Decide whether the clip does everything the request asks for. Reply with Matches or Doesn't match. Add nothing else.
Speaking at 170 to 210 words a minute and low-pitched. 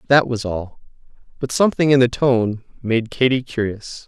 Doesn't match